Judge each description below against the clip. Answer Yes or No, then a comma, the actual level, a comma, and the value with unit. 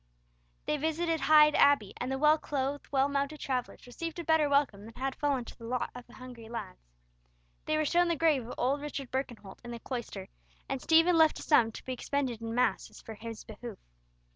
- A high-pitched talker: Yes, very high, 265 Hz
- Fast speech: Yes, fast, 210 wpm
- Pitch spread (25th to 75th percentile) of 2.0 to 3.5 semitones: No, average, 4.3 semitones